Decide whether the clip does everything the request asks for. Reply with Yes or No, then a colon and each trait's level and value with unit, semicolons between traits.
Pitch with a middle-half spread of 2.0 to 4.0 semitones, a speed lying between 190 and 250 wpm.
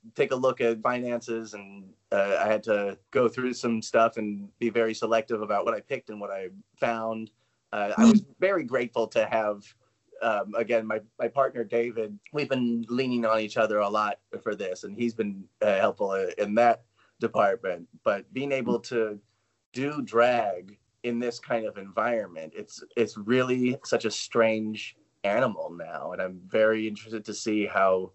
No: average, 2.7 semitones; average, 175 wpm